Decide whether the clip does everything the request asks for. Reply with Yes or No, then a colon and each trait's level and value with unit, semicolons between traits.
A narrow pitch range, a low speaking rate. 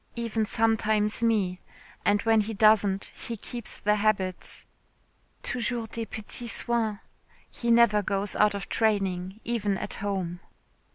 Yes: narrow, 2.1 semitones; slow, 130 wpm